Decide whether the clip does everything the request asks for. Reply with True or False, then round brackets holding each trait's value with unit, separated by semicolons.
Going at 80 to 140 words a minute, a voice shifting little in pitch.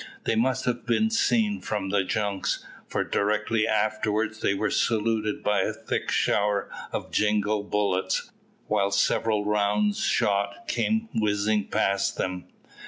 True (135 wpm; 1.7 semitones)